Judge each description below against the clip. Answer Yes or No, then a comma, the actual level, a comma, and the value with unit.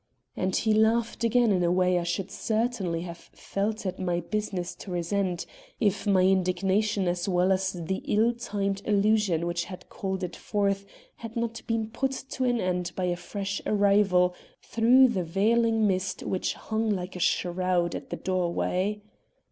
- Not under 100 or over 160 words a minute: No, average, 170 wpm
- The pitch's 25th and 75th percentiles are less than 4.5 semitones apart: Yes, average, 3.2 semitones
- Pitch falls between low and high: No, high, 195 Hz